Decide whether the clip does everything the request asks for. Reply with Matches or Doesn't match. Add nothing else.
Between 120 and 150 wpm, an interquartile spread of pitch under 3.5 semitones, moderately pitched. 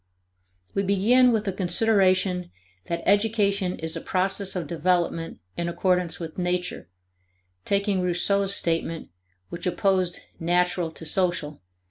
Matches